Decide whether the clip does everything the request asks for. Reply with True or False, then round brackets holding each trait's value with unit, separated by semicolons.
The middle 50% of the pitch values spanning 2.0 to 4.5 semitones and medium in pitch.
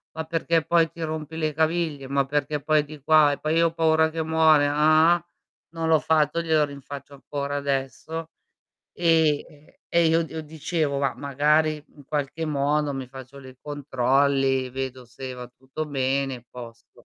True (2.6 semitones; 150 Hz)